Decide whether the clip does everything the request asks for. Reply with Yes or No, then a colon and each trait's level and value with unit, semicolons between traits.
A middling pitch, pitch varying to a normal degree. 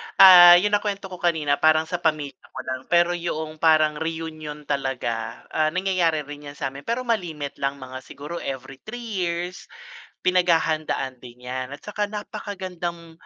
Yes: medium, 160 Hz; average, 4.0 semitones